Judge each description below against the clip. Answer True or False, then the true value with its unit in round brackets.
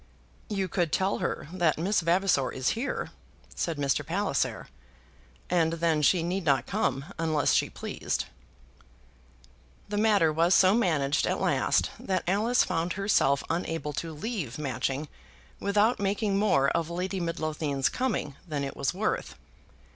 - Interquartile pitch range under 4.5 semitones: False (4.8 semitones)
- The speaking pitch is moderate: True (170 Hz)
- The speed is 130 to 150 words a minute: True (140 wpm)